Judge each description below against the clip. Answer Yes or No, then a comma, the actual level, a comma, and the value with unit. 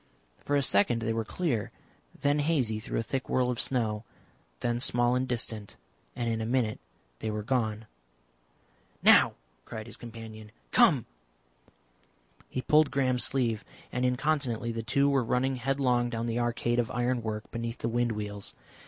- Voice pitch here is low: Yes, low, 120 Hz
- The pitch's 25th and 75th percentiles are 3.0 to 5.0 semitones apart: No, narrow, 2.4 semitones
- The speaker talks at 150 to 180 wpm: Yes, average, 160 wpm